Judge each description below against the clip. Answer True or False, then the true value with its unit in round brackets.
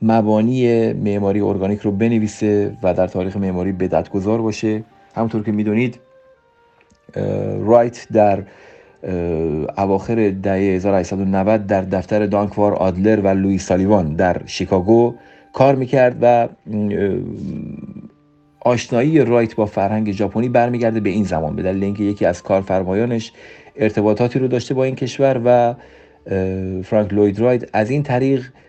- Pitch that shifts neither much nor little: True (3.6 semitones)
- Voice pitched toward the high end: False (105 Hz)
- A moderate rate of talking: True (125 wpm)